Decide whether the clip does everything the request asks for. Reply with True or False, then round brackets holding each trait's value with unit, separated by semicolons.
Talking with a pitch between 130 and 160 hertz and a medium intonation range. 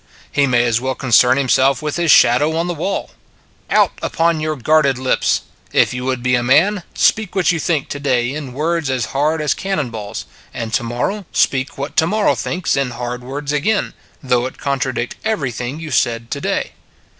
True (140 Hz; 4.3 semitones)